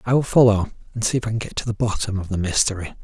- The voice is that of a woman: No, male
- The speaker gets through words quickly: Yes, fast, 295 wpm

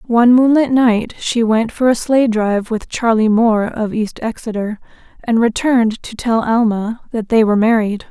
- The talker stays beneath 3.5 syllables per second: No, 4.9 syllables/s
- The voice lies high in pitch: Yes, high, 225 Hz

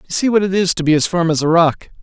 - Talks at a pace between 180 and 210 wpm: No, fast, 355 wpm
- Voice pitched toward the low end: No, medium, 170 Hz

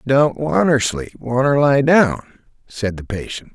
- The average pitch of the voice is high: No, low, 130 Hz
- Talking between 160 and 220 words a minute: No, average, 150 wpm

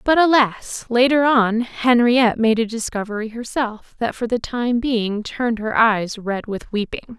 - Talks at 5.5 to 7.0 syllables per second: No, 4.3 syllables/s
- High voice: Yes, high, 230 Hz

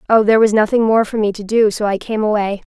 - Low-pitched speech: No, high, 215 Hz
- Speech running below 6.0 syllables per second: No, 6.5 syllables/s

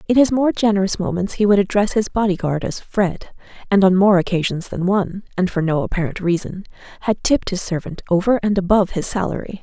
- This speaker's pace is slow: No, average, 200 wpm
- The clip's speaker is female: Yes, female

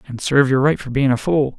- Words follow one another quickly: Yes, fast, 300 wpm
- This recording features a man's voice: Yes, male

